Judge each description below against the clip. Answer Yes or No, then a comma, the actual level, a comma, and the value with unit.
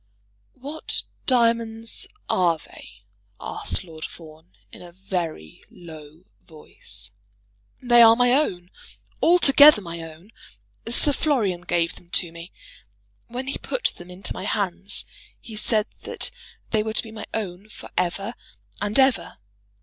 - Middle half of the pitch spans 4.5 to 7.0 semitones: Yes, average, 5.3 semitones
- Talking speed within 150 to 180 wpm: No, slow, 135 wpm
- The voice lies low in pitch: No, high, 195 Hz